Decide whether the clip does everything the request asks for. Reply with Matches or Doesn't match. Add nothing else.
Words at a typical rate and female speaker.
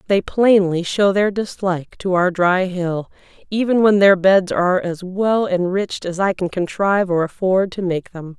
Matches